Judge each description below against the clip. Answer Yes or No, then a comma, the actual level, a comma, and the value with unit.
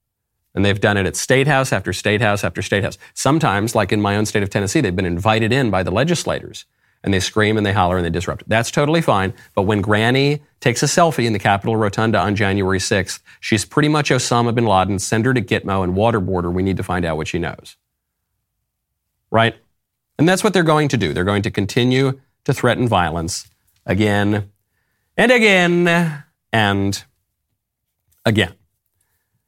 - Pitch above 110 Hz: No, low, 105 Hz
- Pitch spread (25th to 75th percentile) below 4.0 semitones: No, average, 4.4 semitones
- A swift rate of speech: No, average, 195 wpm